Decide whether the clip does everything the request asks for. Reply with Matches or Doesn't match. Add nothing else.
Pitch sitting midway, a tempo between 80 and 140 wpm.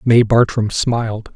Doesn't match